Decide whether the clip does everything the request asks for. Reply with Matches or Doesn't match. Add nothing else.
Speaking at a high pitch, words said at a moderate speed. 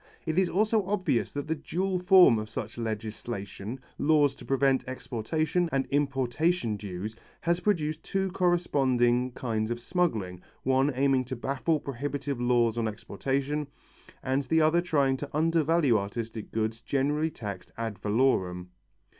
Doesn't match